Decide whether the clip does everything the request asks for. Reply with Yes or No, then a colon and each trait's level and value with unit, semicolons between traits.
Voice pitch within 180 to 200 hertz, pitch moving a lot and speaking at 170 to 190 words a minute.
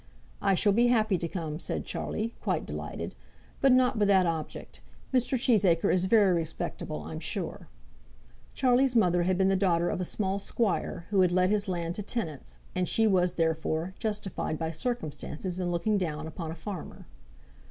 No: medium, 185 Hz; average, 4.1 semitones; average, 175 wpm